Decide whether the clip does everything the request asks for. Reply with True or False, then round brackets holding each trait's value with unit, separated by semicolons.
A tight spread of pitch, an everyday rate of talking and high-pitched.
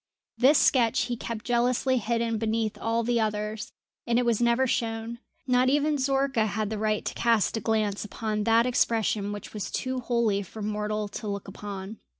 True (2.3 semitones; 180 wpm; 225 Hz)